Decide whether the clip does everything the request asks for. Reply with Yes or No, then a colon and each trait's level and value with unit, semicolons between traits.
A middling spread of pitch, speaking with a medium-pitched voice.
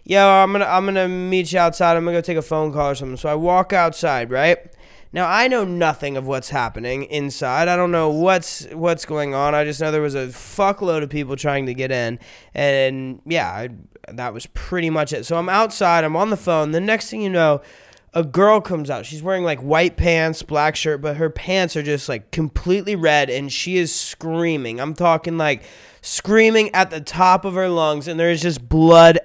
Yes: average, 3.5 semitones; medium, 165 Hz